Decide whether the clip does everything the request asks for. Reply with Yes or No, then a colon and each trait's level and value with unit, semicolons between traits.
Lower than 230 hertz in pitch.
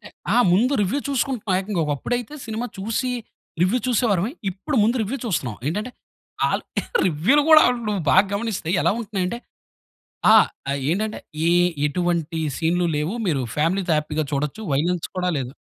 Yes: high, 190 Hz